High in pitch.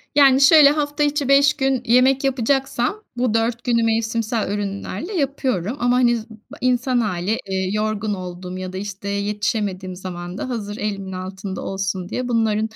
Yes: high, 225 Hz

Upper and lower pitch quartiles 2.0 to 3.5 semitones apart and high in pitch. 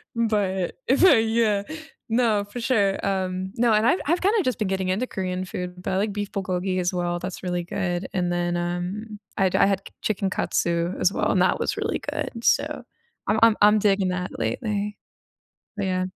Yes: average, 2.9 semitones; high, 195 Hz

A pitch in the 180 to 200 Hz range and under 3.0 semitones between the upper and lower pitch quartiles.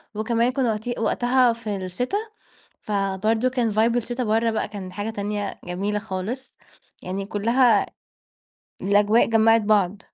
No: high, 220 Hz; narrow, 2.6 semitones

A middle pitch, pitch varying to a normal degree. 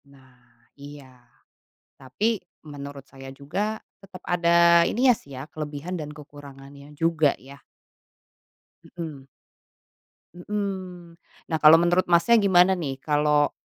Yes: medium, 155 Hz; average, 4.0 semitones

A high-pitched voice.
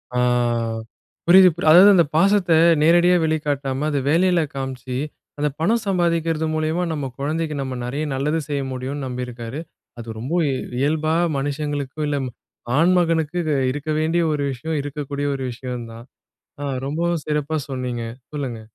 No: medium, 150 Hz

